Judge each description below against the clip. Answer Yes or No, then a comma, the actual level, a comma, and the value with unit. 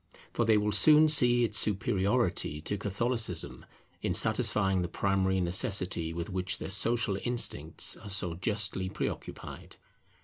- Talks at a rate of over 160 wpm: No, slow, 135 wpm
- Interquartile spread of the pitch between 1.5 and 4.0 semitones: Yes, average, 3.5 semitones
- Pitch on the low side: Yes, low, 100 Hz